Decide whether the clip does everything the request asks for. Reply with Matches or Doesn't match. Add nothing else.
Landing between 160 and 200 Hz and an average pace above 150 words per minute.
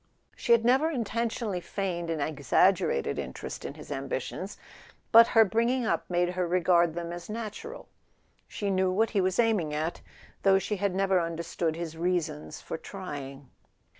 Matches